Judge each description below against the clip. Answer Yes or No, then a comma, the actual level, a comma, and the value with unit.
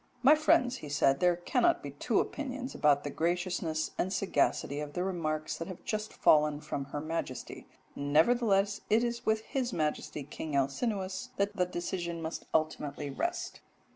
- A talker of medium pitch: Yes, medium, 175 Hz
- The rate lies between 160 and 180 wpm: Yes, average, 165 wpm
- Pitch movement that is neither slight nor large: No, wide, 6.3 semitones